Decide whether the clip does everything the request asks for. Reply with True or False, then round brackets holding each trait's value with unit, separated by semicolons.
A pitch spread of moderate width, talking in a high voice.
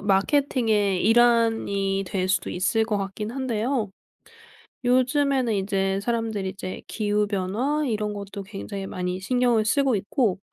True (3.6 semitones; 210 Hz)